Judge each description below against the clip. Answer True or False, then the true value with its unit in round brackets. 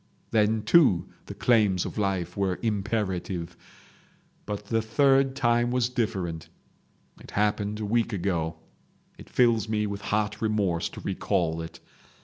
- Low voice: True (105 Hz)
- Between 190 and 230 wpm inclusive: False (135 wpm)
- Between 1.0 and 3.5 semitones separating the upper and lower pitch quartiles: True (3.2 semitones)